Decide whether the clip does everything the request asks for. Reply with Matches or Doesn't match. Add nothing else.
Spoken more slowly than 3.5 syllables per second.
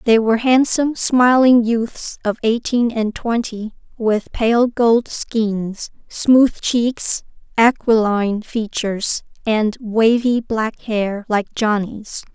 Matches